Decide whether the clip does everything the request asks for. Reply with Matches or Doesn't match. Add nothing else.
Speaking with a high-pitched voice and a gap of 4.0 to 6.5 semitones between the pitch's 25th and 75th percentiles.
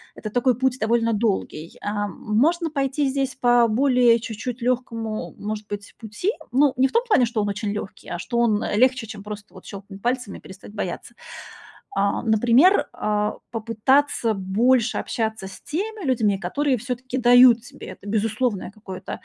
Doesn't match